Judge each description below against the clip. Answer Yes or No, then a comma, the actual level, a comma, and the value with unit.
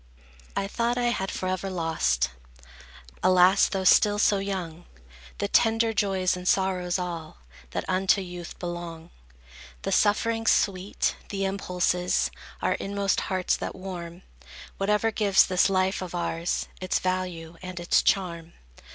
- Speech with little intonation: Yes, narrow, 2.0 semitones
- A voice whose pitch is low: No, medium, 185 Hz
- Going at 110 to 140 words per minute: Yes, slow, 135 wpm